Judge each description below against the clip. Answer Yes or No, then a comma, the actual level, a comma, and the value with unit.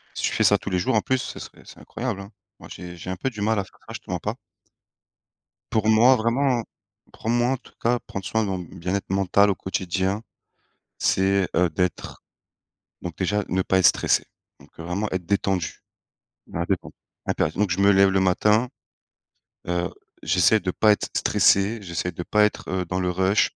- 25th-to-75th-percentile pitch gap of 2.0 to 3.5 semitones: Yes, average, 2.9 semitones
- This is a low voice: Yes, very low, 95 Hz